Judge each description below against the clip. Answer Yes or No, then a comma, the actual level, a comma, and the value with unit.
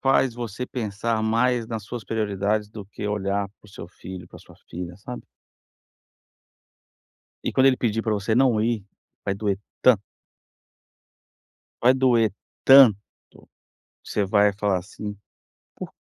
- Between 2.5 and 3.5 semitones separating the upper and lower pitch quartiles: Yes, average, 2.9 semitones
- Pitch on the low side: Yes, low, 110 Hz